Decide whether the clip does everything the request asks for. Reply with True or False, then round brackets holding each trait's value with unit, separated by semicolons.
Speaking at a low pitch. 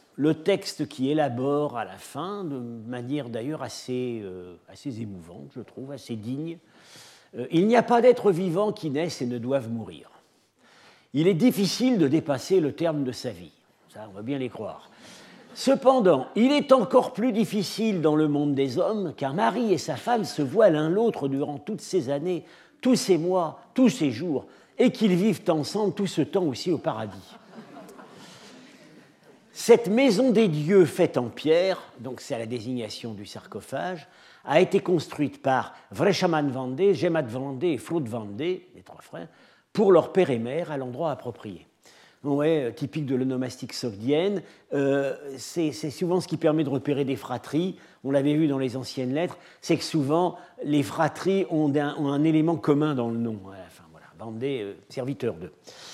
False (150 Hz)